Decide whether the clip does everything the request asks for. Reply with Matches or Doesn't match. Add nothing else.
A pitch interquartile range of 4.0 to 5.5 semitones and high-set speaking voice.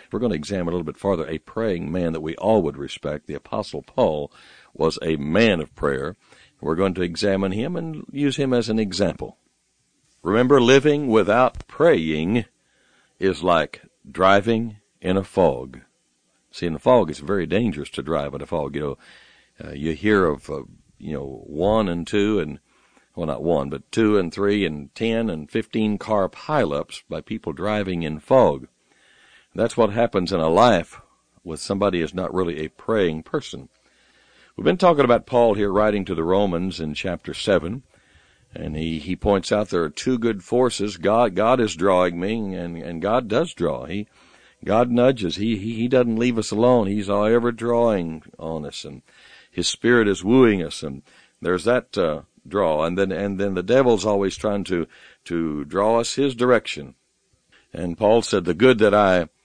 Doesn't match